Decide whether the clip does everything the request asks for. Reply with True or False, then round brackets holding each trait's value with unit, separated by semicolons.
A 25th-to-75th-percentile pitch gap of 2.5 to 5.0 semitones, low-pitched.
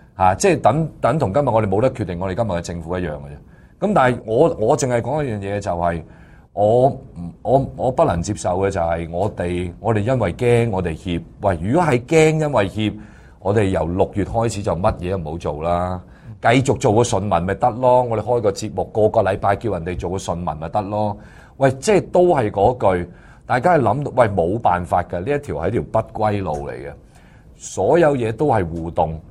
False (5.6 semitones; 105 Hz)